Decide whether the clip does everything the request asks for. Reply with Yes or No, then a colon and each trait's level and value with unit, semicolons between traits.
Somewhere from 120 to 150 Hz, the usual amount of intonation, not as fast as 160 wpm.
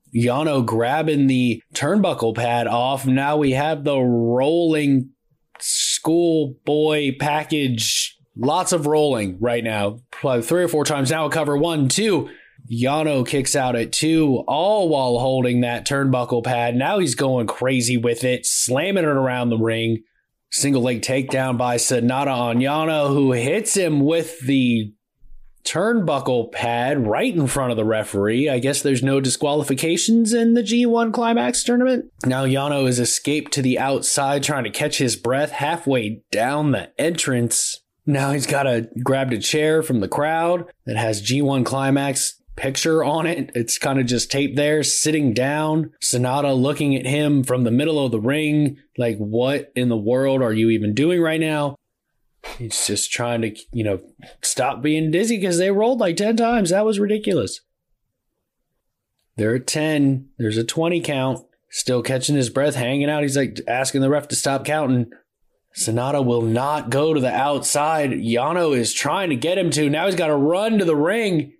No: low, 135 Hz; average, 3.7 semitones; average, 170 wpm